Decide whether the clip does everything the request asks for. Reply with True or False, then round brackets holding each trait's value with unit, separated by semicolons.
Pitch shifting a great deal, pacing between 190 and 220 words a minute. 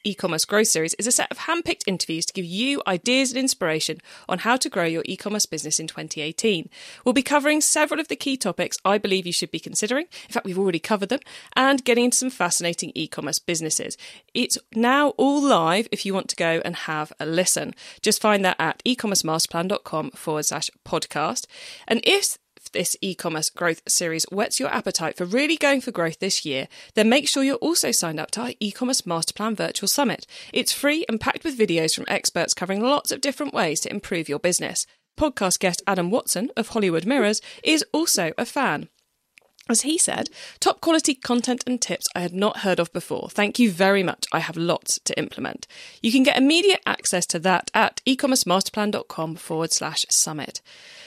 True (7.0 semitones; 195 wpm)